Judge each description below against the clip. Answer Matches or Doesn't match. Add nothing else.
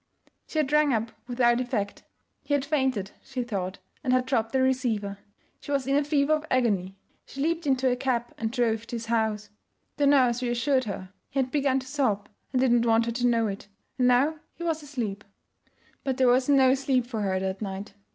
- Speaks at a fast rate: Matches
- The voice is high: Matches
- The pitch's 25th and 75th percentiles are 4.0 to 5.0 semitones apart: Doesn't match